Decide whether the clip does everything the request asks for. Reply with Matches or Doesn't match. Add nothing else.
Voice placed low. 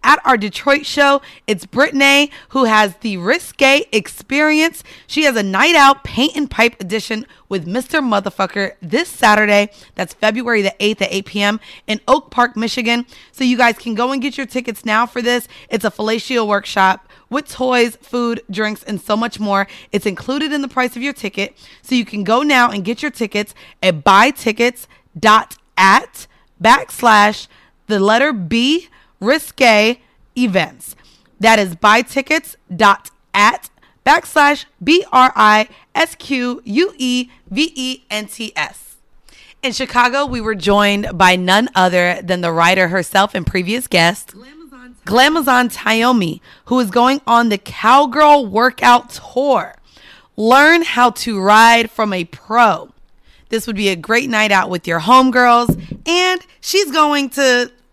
Doesn't match